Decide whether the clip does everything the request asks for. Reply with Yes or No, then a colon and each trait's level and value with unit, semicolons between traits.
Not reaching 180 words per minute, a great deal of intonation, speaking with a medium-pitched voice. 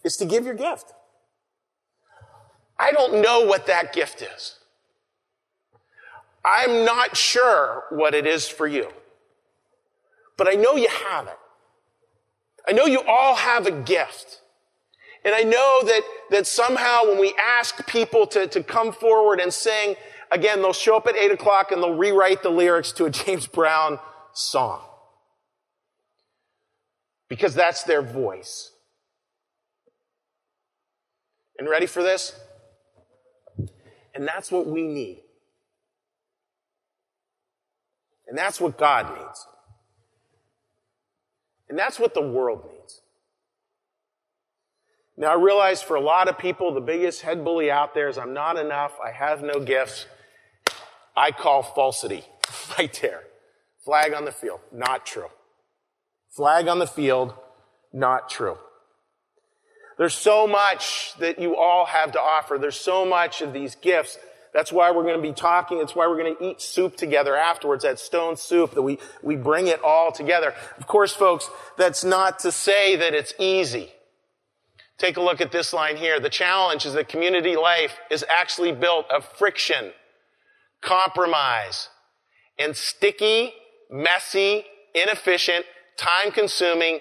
Yes: average, 140 wpm; wide, 6.7 semitones; medium, 180 Hz